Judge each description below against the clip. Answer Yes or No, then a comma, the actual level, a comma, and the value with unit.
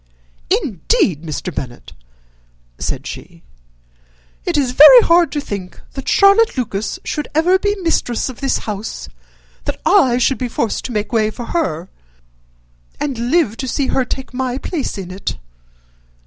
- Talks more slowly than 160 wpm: Yes, average, 150 wpm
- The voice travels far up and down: Yes, wide, 6.4 semitones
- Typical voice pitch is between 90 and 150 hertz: No, very high, 255 Hz